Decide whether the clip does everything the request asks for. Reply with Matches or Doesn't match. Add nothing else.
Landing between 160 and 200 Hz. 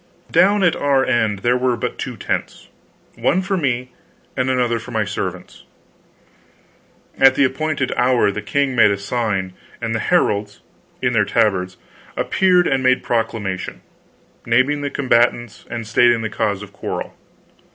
Doesn't match